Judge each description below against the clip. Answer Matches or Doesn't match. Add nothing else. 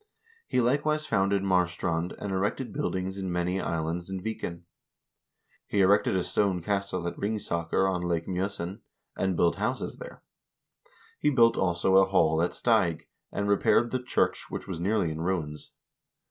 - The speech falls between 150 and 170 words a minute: Matches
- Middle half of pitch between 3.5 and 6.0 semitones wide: Doesn't match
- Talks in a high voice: Doesn't match